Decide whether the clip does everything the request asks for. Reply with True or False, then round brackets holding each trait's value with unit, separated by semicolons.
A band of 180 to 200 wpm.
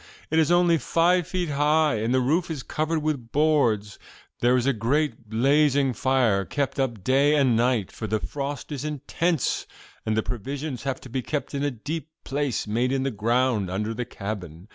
True (190 wpm)